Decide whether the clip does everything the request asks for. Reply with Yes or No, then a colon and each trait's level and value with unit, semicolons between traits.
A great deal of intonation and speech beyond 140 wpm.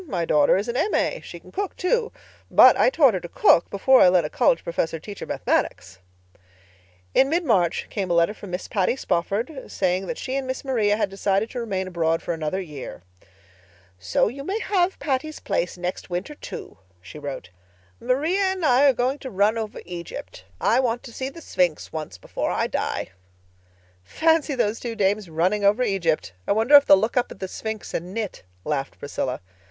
Yes: wide, 7.1 semitones; average, 200 wpm